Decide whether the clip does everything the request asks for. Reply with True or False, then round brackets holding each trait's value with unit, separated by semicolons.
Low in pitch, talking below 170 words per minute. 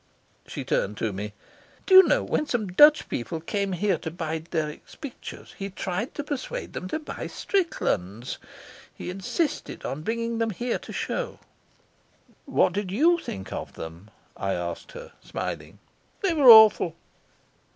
False (195 Hz; 150 wpm)